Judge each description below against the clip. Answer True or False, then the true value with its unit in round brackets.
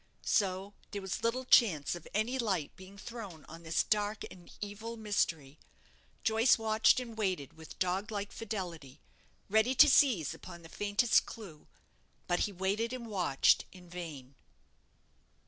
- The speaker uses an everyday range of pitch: True (4.4 semitones)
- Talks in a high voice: True (200 Hz)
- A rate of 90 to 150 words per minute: True (145 wpm)